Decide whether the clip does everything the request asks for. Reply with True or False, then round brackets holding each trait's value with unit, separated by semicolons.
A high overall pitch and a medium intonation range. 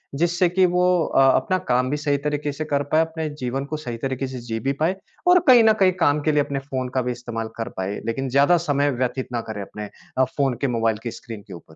False (135 Hz; 3.9 semitones)